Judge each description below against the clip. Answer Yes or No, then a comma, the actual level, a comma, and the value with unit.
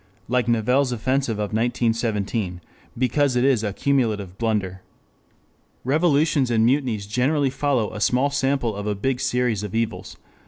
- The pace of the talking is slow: No, average, 150 wpm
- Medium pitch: No, low, 120 Hz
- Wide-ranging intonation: No, average, 4.0 semitones